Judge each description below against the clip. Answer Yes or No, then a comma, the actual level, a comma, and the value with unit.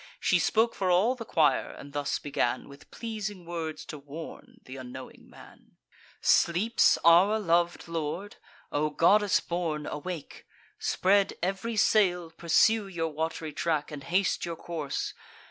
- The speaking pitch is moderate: Yes, medium, 170 Hz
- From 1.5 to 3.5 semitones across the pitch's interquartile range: No, average, 4.4 semitones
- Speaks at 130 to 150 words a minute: Yes, average, 140 wpm